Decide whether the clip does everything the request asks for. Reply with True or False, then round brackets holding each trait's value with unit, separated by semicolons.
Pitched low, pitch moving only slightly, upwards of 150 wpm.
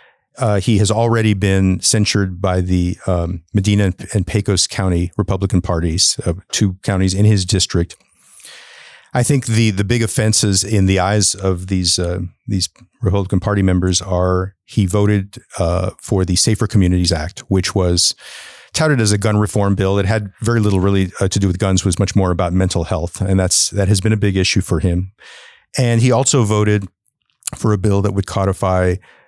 True (100 Hz; 2.3 semitones; 190 wpm)